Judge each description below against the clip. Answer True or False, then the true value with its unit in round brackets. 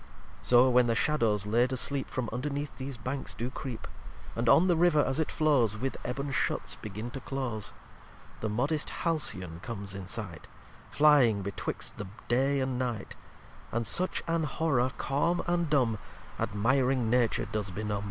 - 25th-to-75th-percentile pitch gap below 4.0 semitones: False (4.4 semitones)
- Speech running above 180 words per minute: False (160 wpm)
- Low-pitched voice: True (125 Hz)